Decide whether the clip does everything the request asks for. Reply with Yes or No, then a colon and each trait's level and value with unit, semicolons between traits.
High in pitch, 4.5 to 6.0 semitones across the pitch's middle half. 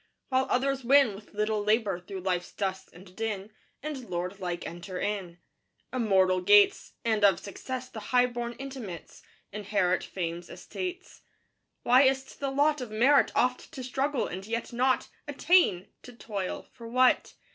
Yes: high, 220 Hz; average, 5.3 semitones